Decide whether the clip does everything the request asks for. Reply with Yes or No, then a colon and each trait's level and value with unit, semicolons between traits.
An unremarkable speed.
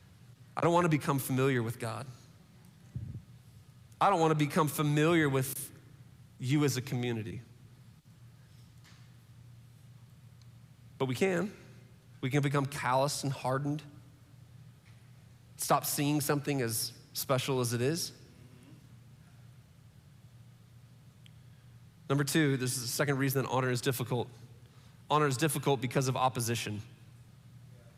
No: slow, 115 wpm